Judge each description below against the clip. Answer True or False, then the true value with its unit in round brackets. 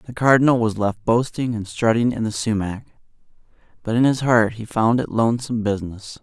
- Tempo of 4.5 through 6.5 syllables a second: True (5.5 syllables/s)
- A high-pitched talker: False (115 Hz)